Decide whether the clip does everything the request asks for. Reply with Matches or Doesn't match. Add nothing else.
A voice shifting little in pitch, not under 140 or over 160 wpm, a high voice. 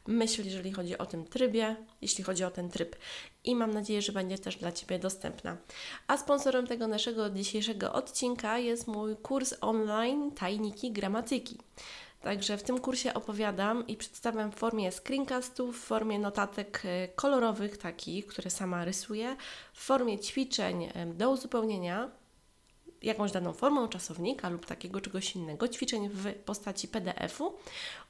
Doesn't match